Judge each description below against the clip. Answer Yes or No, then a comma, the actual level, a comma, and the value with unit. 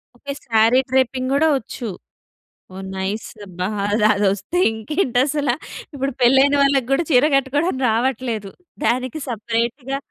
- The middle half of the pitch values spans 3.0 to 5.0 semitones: Yes, average, 3.7 semitones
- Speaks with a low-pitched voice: No, very high, 255 Hz